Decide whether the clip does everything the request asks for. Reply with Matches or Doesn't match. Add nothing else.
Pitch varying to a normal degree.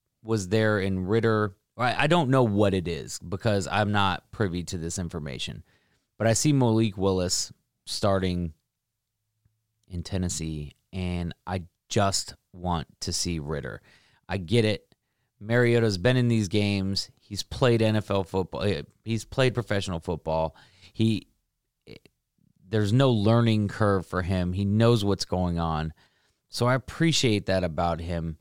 Matches